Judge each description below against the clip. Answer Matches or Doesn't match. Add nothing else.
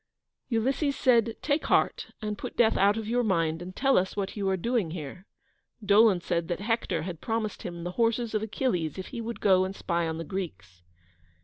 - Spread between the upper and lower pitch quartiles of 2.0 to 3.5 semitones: Doesn't match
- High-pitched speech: Matches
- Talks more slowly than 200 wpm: Doesn't match